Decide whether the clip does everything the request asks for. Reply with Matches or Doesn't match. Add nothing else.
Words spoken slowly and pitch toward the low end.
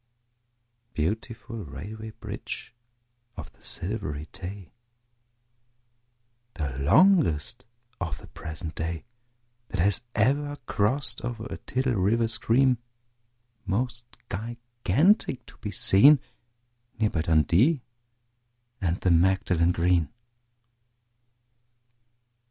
Matches